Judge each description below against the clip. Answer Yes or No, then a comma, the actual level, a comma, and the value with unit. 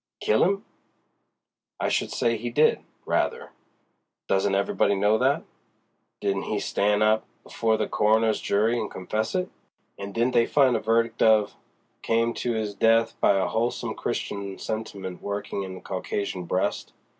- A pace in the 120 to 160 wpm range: Yes, average, 155 wpm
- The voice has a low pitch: Yes, low, 110 Hz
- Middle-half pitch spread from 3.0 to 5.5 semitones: No, narrow, 2.4 semitones